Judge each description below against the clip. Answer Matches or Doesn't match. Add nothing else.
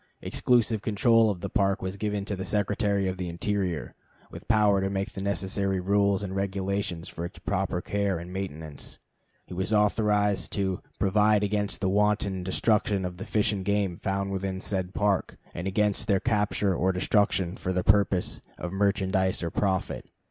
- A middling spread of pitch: Doesn't match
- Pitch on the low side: Matches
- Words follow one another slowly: Doesn't match